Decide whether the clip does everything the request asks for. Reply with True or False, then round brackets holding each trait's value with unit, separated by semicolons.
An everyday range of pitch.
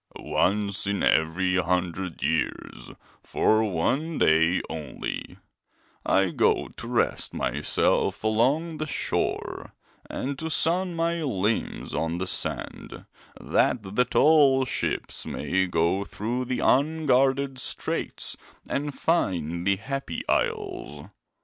False (7.9 semitones)